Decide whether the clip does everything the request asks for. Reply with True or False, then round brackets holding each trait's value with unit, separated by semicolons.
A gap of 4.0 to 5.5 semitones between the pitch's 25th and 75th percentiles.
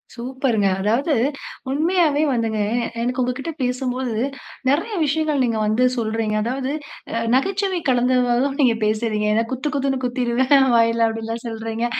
False (3.1 semitones)